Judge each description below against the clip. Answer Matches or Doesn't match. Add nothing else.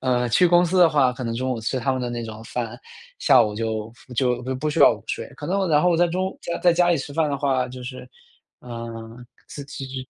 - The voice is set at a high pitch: Doesn't match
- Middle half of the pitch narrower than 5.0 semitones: Doesn't match